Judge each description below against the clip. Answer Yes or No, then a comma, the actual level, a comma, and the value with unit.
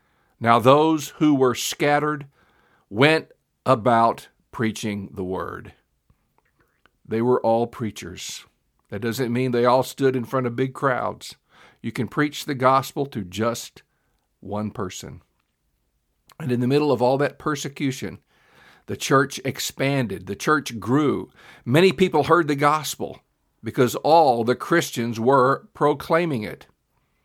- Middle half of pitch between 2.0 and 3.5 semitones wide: No, average, 4.3 semitones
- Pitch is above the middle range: No, low, 130 Hz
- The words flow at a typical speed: No, slow, 130 wpm